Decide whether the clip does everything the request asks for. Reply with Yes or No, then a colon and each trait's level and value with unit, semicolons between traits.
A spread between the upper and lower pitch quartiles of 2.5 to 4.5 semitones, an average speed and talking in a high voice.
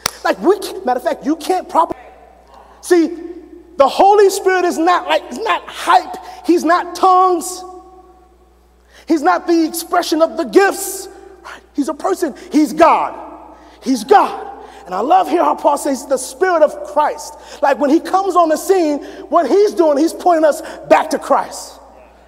Yes: average, 3.0 semitones; average, 165 wpm; very high, 345 Hz